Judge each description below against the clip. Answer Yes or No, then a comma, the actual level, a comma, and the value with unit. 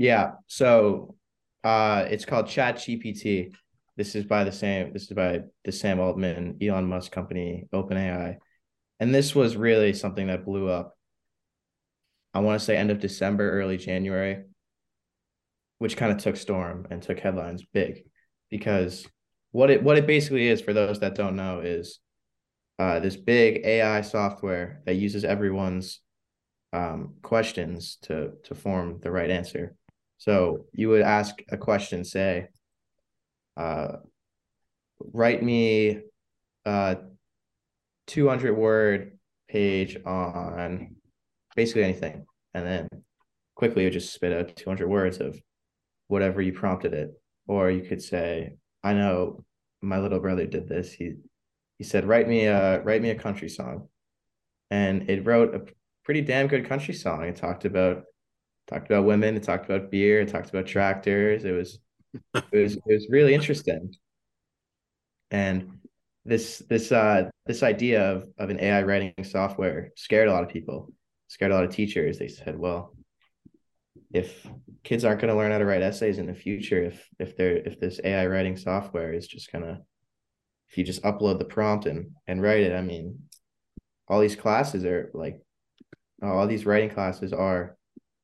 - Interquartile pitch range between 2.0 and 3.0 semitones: Yes, average, 2.7 semitones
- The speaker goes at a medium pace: Yes, average, 160 wpm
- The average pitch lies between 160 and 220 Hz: No, low, 100 Hz